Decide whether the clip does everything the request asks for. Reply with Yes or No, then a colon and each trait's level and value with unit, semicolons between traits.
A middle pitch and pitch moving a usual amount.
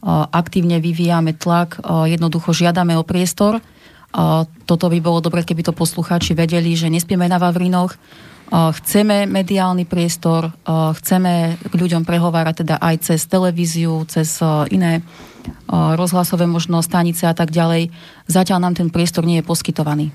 No: medium, 170 Hz; narrow, 1.4 semitones